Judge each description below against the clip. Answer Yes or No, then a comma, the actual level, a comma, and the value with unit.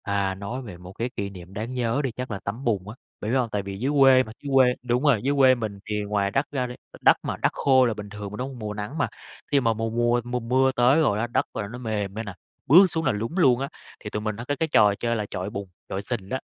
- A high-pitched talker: No, low, 115 Hz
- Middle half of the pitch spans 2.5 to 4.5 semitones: Yes, average, 3.9 semitones